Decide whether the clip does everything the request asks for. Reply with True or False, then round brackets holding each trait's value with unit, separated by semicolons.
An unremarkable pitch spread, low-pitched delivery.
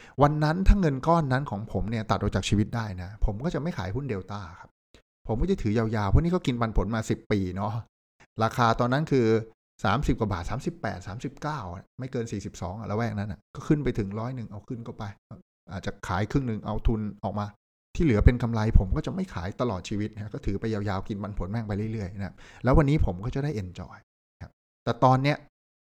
True (4.0 semitones; 110 Hz)